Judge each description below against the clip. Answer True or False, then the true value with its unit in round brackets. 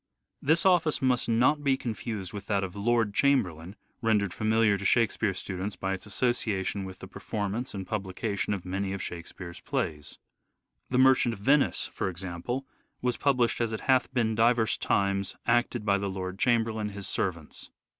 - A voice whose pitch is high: False (105 Hz)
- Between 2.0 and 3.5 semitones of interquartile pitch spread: False (4.0 semitones)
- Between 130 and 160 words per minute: False (170 wpm)